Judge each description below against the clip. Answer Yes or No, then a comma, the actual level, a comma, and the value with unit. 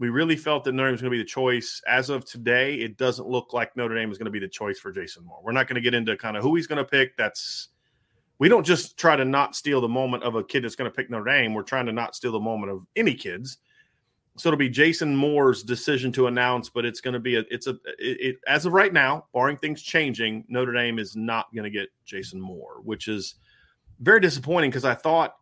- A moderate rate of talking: No, fast, 265 wpm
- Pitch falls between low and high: No, low, 125 Hz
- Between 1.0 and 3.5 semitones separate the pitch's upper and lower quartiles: Yes, average, 3.1 semitones